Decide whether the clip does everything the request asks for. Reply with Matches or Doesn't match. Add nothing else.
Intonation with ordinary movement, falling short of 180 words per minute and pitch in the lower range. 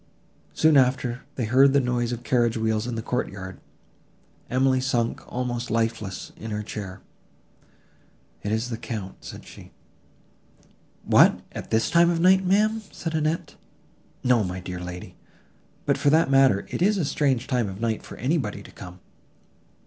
Matches